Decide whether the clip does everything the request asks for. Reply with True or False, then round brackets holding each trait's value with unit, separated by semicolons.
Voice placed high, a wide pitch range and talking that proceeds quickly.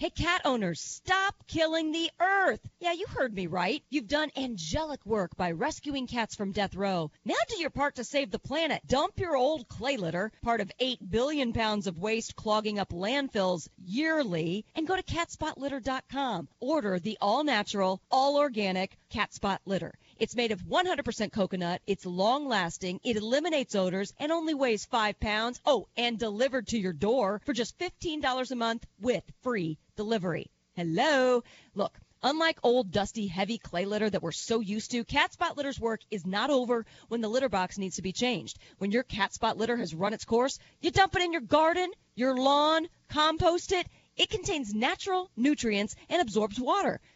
False (235 Hz; 6.5 semitones; 180 wpm)